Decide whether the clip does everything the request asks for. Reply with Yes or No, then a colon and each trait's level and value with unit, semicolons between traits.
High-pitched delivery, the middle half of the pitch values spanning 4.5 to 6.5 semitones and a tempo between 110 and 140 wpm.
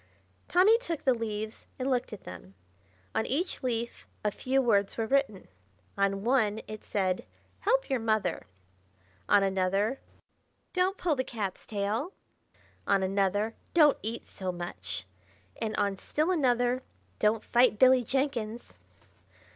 Yes: high, 225 Hz; average, 4.9 semitones; slow, 135 wpm